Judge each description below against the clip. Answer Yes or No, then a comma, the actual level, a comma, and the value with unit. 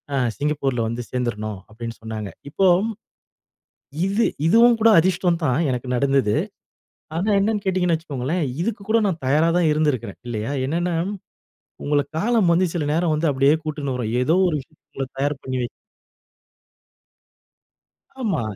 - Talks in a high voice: No, medium, 150 Hz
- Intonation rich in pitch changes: Yes, wide, 5.8 semitones